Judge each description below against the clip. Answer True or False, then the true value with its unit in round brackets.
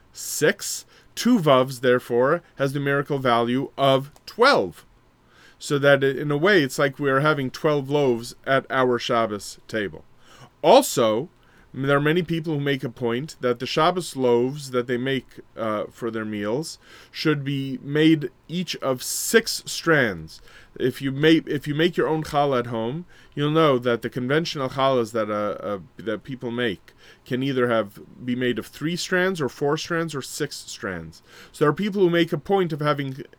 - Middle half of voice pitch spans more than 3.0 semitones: True (3.7 semitones)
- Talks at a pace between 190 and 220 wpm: False (180 wpm)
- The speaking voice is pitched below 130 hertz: False (135 Hz)